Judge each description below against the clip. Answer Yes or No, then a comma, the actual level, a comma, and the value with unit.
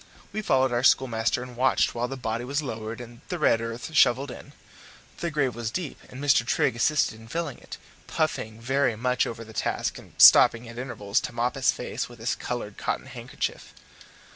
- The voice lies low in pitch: Yes, low, 120 Hz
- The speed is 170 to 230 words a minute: Yes, average, 195 wpm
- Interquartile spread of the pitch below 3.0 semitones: Yes, narrow, 2.6 semitones